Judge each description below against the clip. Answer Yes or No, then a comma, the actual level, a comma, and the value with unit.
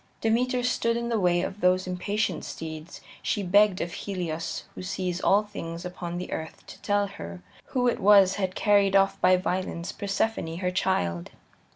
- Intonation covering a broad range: No, average, 2.8 semitones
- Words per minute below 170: No, average, 175 wpm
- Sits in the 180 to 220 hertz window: Yes, medium, 185 Hz